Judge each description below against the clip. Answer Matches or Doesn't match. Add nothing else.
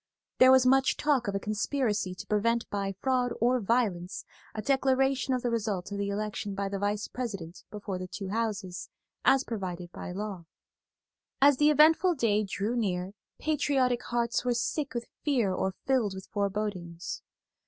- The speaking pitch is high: Matches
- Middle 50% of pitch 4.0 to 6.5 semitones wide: Matches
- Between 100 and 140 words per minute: Doesn't match